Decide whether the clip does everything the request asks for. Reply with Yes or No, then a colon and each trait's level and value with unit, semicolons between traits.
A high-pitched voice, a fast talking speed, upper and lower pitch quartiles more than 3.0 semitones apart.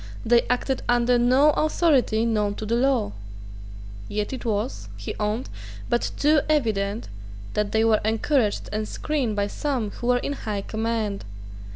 No: high, 230 Hz; average, 155 wpm; average, 3.5 semitones